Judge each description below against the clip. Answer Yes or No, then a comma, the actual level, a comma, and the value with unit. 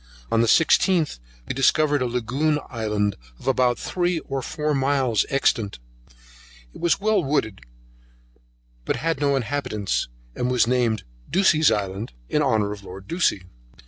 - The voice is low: Yes, low, 130 Hz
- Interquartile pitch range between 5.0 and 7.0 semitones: Yes, wide, 5.6 semitones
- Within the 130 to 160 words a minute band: Yes, average, 145 wpm